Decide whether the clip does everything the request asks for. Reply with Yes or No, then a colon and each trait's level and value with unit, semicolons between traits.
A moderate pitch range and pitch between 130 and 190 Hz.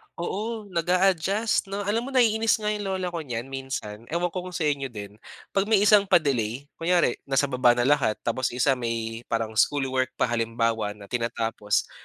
No: wide, 8.3 semitones; medium, 140 Hz